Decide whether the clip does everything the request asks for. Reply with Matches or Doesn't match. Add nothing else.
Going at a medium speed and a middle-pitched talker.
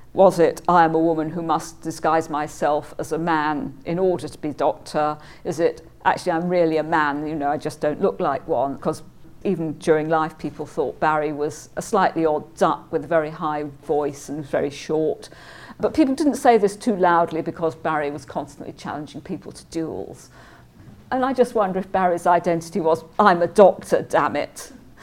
Matches